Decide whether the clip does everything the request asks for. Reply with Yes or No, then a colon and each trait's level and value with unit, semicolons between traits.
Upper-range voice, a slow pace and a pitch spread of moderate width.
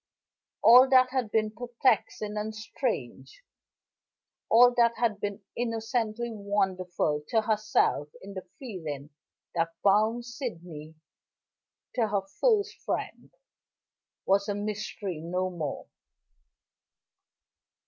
Yes: high, 215 Hz; slow, 100 wpm; average, 4.3 semitones